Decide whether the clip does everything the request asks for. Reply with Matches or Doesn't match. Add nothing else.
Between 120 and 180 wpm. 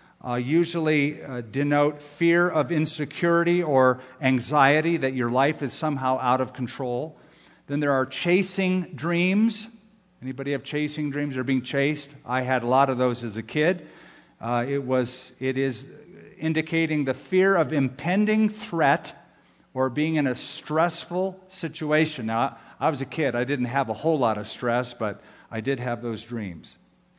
Matches